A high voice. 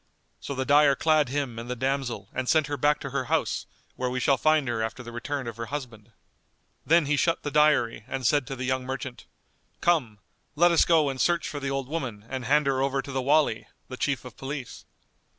No: low, 135 Hz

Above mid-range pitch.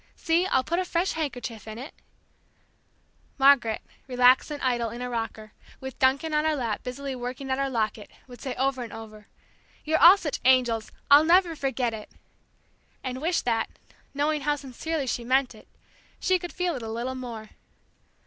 Yes: very high, 260 Hz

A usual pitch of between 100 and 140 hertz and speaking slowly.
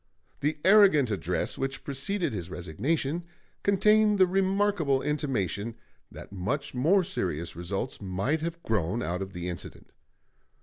Yes: low, 135 Hz; slow, 130 wpm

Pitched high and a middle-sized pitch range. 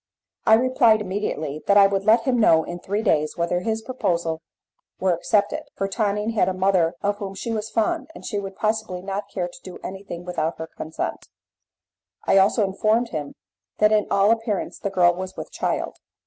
Yes: high, 195 Hz; average, 3.3 semitones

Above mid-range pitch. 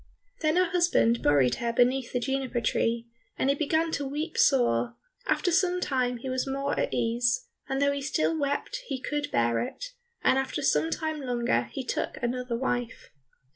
Yes: very high, 270 Hz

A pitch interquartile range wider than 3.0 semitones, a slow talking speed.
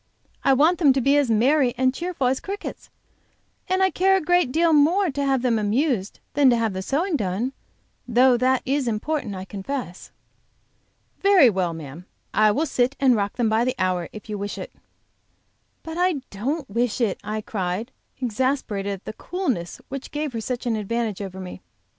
No: wide, 5.6 semitones; average, 190 wpm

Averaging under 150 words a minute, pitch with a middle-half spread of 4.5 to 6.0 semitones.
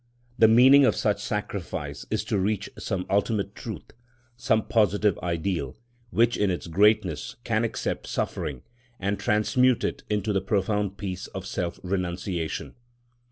No: average, 140 wpm; average, 2.8 semitones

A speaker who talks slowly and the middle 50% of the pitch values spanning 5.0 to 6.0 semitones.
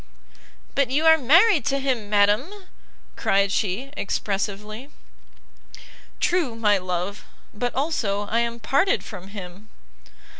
Yes: slow, 115 wpm; average, 5.3 semitones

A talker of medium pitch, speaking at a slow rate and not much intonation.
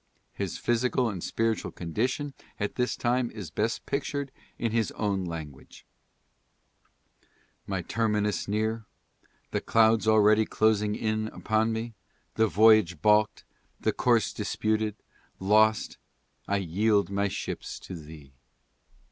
No: low, 110 Hz; slow, 120 wpm; narrow, 1.9 semitones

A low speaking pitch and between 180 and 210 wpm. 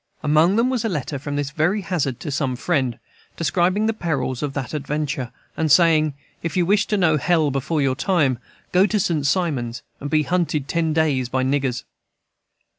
No: medium, 155 Hz; average, 190 wpm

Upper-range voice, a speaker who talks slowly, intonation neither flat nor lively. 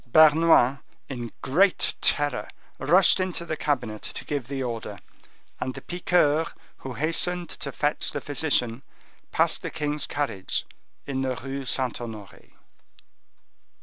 No: medium, 140 Hz; slow, 130 wpm; average, 4.0 semitones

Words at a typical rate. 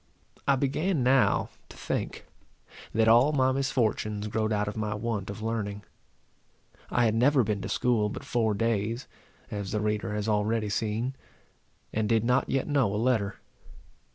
Yes: average, 160 wpm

